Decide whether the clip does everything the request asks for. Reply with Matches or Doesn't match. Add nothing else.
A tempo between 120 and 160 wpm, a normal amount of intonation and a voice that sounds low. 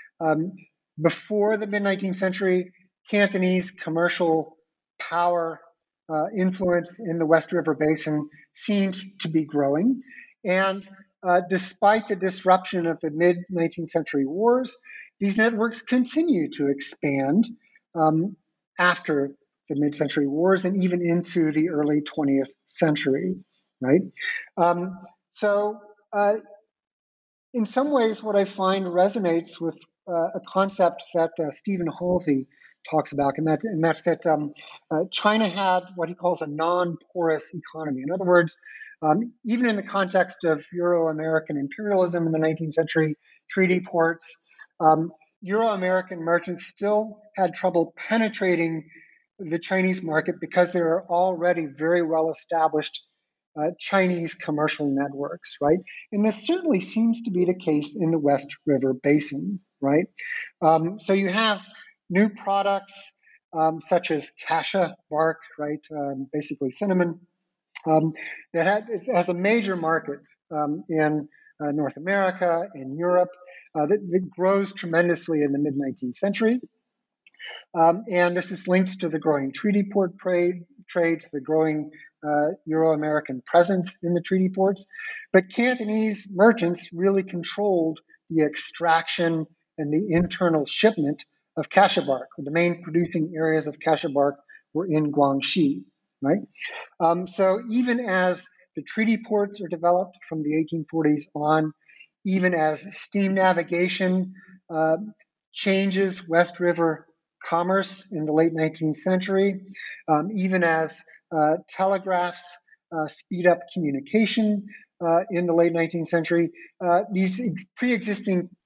Doesn't match